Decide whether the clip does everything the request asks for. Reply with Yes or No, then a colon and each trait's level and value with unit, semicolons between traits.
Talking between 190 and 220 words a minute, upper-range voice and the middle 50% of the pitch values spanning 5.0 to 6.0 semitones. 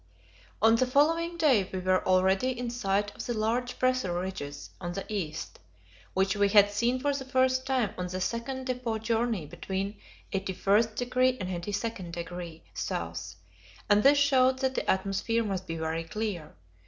No: average, 160 wpm; high, 210 Hz; wide, 5.4 semitones